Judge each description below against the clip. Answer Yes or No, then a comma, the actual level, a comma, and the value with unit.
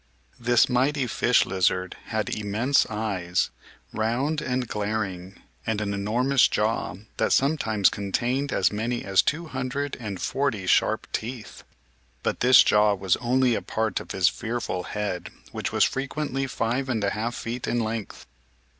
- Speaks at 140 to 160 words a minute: Yes, average, 150 wpm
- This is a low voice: Yes, low, 115 Hz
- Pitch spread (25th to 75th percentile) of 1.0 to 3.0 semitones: No, average, 4.0 semitones